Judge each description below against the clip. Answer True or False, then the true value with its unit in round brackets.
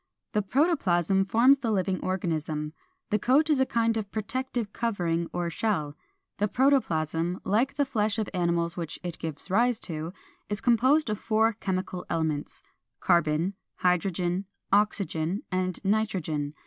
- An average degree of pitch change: True (4.9 semitones)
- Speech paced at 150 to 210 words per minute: False (140 wpm)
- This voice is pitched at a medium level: False (195 Hz)